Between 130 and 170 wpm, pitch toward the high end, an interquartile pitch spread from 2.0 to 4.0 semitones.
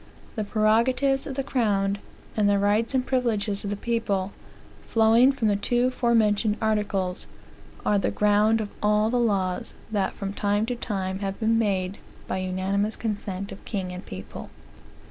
Yes: average, 165 wpm; high, 210 Hz; narrow, 2.4 semitones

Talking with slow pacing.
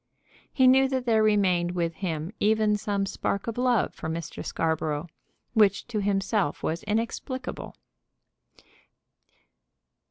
Yes: slow, 120 wpm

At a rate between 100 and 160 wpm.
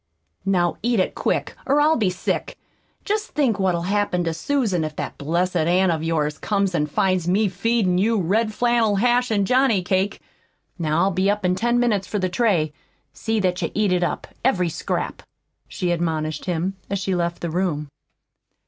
No: average, 185 wpm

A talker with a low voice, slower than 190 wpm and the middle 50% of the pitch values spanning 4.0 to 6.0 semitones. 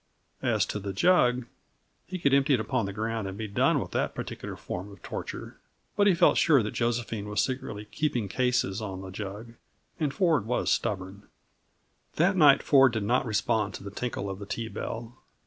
No: low, 115 Hz; average, 195 wpm; average, 4.8 semitones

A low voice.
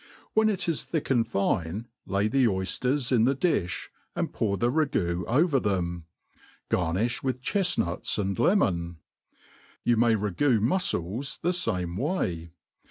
Yes: low, 115 Hz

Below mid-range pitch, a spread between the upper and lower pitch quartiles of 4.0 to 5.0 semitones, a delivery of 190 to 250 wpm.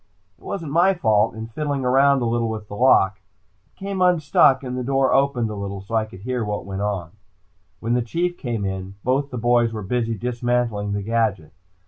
Yes: low, 120 Hz; average, 4.4 semitones; fast, 205 wpm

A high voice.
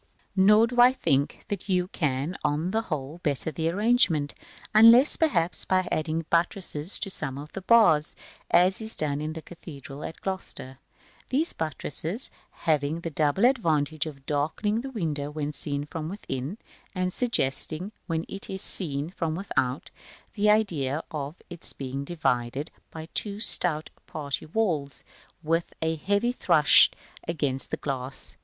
No: medium, 160 Hz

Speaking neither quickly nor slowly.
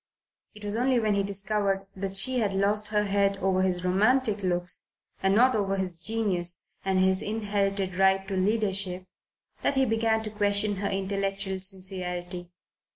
Yes: average, 160 wpm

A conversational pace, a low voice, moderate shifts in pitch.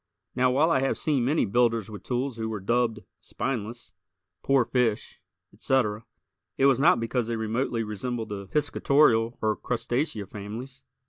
Yes: average, 150 wpm; low, 120 Hz; average, 3.1 semitones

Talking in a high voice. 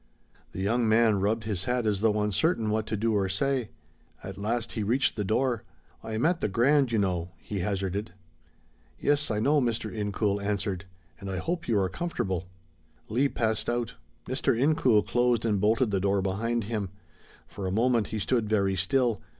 No: low, 110 Hz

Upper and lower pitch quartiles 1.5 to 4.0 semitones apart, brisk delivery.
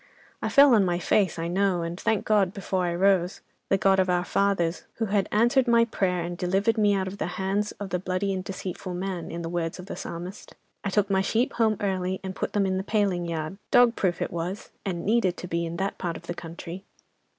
Yes: narrow, 2.4 semitones; fast, 230 wpm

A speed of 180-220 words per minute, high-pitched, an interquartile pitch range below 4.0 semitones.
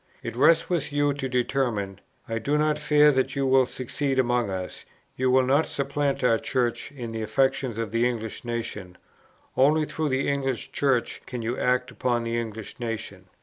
No: average, 185 wpm; low, 130 Hz; average, 3.2 semitones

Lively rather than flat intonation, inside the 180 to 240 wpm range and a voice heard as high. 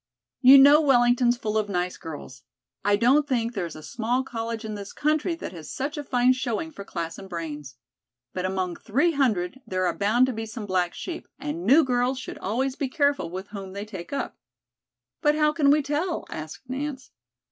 Yes: wide, 6.6 semitones; average, 200 wpm; high, 240 Hz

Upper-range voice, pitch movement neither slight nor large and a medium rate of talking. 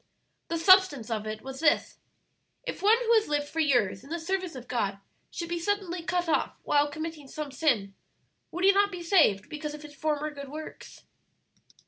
Yes: very high, 305 Hz; average, 4.3 semitones; average, 190 wpm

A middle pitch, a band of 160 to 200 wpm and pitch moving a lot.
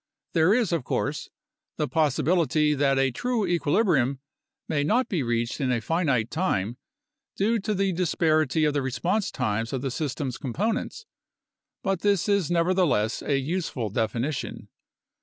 No: medium, 155 Hz; average, 150 wpm; wide, 6.1 semitones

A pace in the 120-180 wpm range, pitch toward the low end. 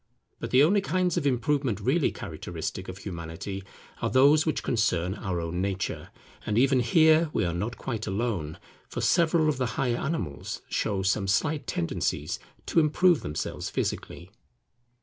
Yes: average, 155 wpm; low, 115 Hz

